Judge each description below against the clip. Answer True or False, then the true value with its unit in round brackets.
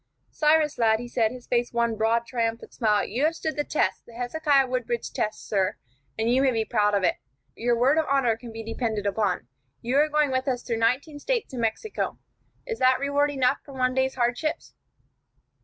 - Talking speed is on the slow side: False (205 wpm)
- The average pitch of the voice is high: True (245 Hz)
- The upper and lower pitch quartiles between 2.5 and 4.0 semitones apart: True (3.7 semitones)